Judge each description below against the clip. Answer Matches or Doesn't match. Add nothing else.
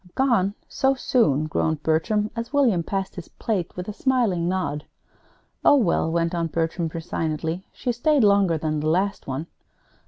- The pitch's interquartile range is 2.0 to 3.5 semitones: Doesn't match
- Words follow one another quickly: Doesn't match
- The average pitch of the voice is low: Doesn't match